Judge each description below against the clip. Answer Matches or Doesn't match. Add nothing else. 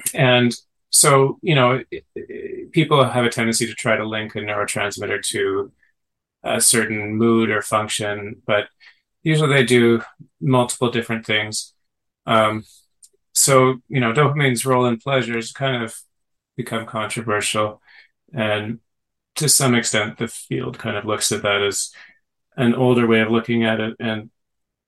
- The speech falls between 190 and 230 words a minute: Doesn't match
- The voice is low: Matches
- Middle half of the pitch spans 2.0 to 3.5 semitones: Matches